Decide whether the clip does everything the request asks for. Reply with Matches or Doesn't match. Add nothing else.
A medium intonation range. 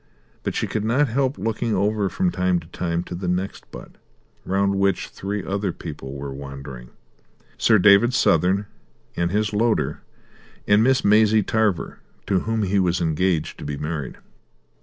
Matches